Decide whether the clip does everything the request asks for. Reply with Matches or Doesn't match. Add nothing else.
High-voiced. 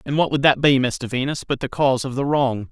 Doesn't match